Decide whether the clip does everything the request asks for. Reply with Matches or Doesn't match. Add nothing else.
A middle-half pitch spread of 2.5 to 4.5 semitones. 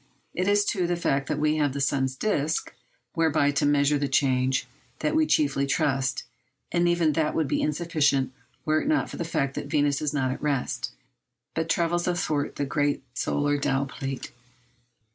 Matches